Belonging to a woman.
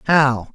No: male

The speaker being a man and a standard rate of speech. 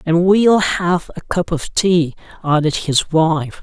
Yes: male; average, 165 wpm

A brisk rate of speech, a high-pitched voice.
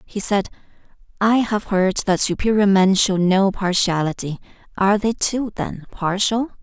No: average, 145 wpm; high, 200 Hz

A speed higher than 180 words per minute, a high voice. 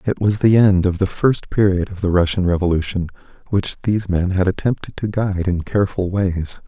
No: average, 200 wpm; very low, 95 Hz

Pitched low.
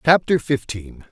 Yes: low, 125 Hz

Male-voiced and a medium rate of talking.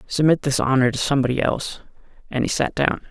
Yes: male; average, 195 wpm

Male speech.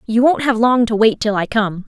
No: female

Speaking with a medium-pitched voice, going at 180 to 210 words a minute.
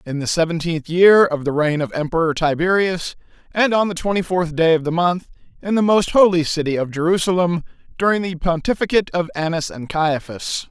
Yes: medium, 170 Hz; average, 185 wpm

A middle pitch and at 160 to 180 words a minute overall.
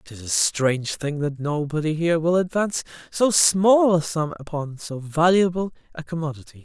Yes: medium, 160 Hz; average, 165 wpm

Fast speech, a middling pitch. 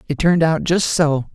Yes: fast, 220 wpm; medium, 150 Hz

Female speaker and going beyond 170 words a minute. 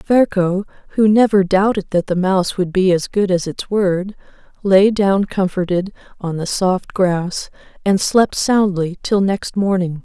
No: female; average, 160 wpm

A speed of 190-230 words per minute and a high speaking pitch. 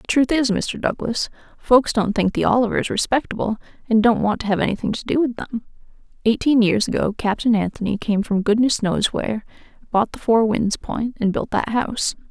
Yes: average, 195 wpm; high, 225 Hz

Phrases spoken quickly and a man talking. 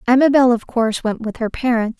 No: fast, 210 wpm; female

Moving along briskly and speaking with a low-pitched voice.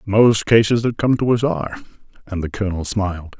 No: average, 195 wpm; low, 105 Hz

